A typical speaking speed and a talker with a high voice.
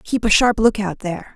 No: fast, 220 wpm; high, 210 Hz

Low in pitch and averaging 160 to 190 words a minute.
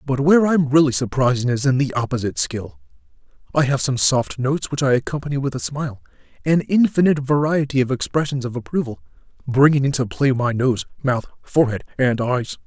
Yes: low, 130 Hz; average, 170 wpm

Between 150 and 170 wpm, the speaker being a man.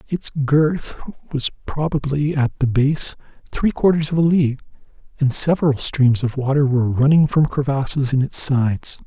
Yes: average, 160 wpm; male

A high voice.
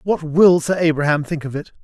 No: medium, 160 Hz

